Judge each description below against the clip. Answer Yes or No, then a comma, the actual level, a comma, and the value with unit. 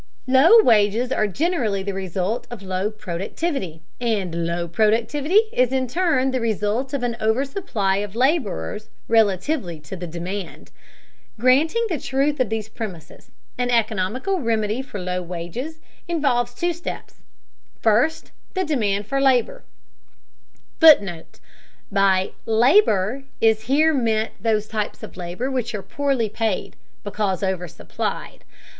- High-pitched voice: Yes, high, 225 Hz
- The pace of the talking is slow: Yes, slow, 130 wpm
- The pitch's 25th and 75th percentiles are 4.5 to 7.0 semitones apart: Yes, wide, 5.4 semitones